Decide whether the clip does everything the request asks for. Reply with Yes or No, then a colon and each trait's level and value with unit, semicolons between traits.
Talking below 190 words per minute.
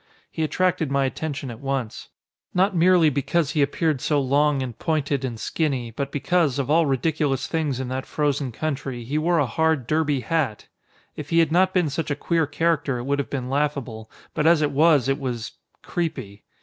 No: average, 195 wpm